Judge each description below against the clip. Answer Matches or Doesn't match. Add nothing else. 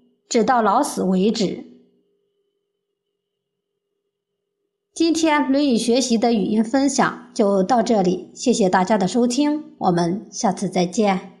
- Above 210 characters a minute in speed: Doesn't match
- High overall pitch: Matches